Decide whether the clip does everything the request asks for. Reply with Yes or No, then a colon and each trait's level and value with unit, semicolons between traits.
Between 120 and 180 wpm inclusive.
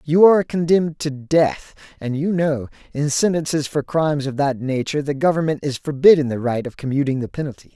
No: average, 195 wpm